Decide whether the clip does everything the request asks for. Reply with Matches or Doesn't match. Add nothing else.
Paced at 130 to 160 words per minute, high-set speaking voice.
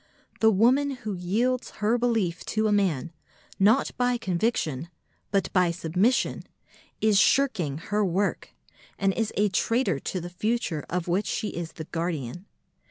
Matches